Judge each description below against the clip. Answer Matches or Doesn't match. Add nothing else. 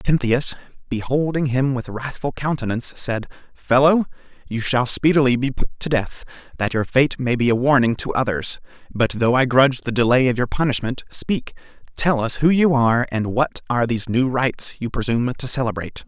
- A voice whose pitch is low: Matches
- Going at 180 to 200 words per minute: Matches